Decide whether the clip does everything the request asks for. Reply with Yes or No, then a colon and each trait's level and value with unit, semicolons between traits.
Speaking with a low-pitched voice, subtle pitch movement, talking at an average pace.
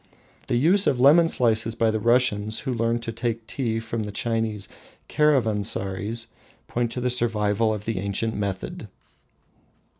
Yes: low, 115 Hz; narrow, 2.2 semitones; average, 150 wpm